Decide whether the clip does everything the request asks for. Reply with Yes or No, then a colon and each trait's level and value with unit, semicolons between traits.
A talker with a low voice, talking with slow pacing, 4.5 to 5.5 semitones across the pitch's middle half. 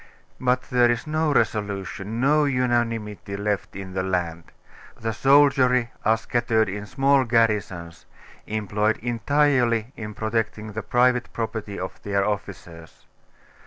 No: low, 110 Hz; slow, 125 wpm; average, 3.5 semitones